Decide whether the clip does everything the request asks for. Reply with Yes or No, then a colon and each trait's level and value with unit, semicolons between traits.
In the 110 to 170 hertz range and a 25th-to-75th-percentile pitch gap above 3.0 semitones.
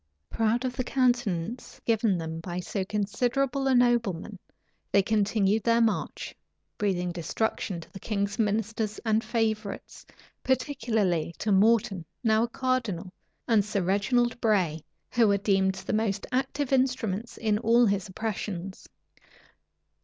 No: high, 215 Hz; average, 3.5 semitones